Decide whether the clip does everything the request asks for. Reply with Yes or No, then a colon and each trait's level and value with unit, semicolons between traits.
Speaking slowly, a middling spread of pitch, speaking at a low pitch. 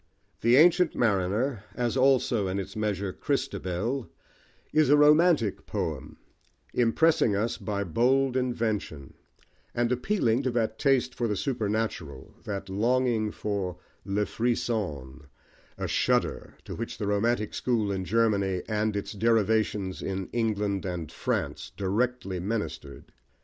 Yes: slow, 125 wpm; average, 3.9 semitones; low, 110 Hz